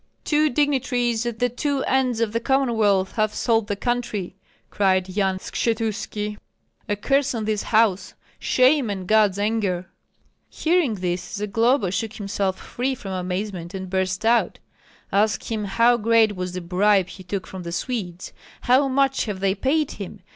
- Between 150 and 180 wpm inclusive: Yes, average, 160 wpm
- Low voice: No, high, 215 Hz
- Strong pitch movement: No, average, 4.2 semitones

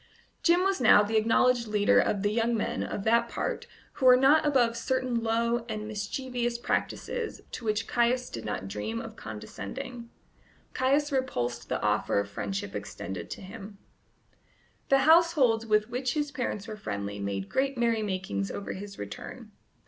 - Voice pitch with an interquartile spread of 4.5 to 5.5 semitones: Yes, average, 5.2 semitones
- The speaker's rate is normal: Yes, average, 160 wpm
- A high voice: Yes, high, 225 Hz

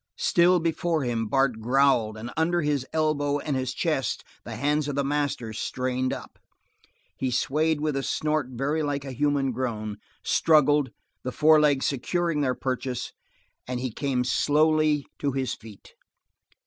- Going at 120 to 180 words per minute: Yes, average, 150 wpm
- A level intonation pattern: No, average, 3.1 semitones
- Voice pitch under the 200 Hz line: Yes, medium, 140 Hz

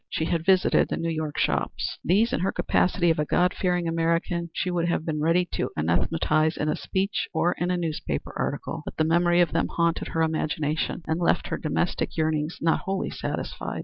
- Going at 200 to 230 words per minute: Yes, fast, 205 wpm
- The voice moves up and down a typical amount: No, narrow, 1.9 semitones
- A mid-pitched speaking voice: Yes, medium, 165 Hz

